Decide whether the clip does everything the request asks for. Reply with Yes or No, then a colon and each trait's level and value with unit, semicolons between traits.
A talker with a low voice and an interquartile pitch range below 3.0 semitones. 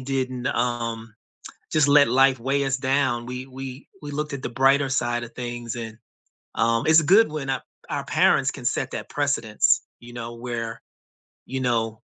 Yes: low, 125 Hz; narrow, 2.5 semitones